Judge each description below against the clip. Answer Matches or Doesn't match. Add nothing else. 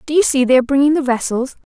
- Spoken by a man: Doesn't match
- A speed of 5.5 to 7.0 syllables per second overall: Doesn't match